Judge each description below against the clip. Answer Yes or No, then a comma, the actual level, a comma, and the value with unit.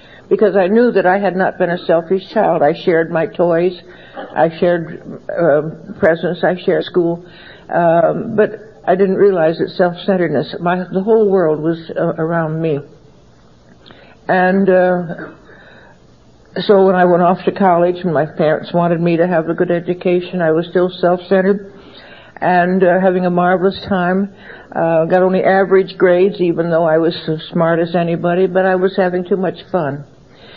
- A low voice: No, medium, 180 Hz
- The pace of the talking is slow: No, average, 170 wpm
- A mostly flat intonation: Yes, narrow, 2.3 semitones